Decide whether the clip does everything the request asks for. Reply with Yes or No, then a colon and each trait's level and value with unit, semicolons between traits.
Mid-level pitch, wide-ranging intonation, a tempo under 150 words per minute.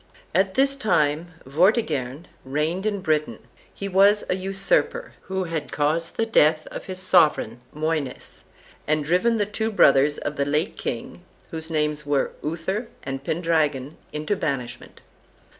No: medium, 160 Hz; average, 4.3 semitones; average, 140 wpm